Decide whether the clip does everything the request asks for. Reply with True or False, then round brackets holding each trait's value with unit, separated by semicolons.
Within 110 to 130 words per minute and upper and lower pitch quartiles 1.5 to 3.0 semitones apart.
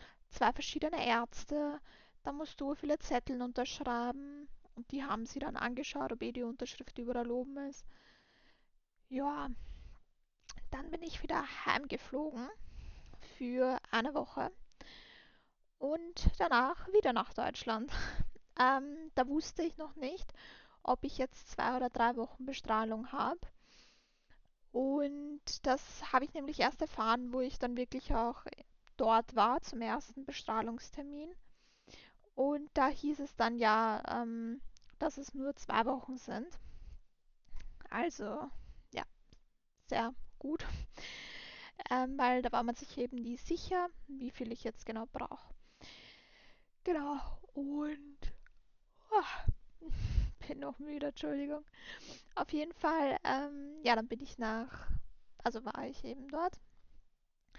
False (125 wpm; 3.4 semitones)